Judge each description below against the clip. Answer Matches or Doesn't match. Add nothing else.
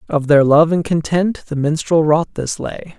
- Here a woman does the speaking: Doesn't match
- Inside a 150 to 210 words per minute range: Matches